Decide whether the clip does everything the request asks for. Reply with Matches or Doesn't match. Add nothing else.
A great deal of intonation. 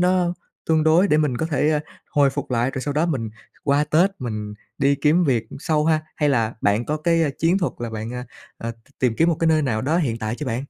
Doesn't match